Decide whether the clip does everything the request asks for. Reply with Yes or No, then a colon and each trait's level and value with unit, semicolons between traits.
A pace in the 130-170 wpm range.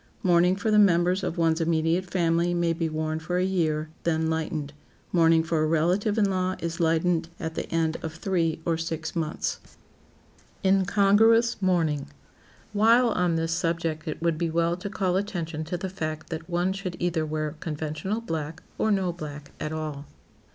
No: average, 180 wpm